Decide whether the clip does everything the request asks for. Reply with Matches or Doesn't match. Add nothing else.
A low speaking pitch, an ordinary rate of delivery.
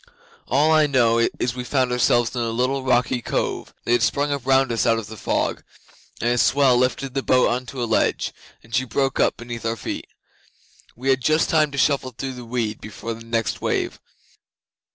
Doesn't match